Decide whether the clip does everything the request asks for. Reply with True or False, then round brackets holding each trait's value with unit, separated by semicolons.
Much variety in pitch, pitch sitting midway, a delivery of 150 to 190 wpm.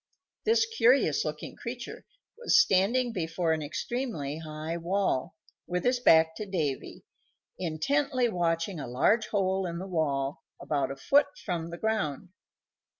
False (6.9 semitones; 180 Hz; 140 wpm)